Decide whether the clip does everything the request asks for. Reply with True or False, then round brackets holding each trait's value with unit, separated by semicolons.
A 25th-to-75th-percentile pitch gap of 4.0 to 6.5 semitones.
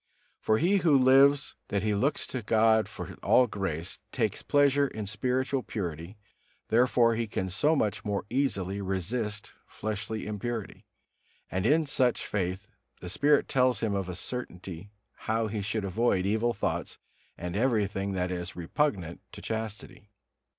True (4.5 semitones)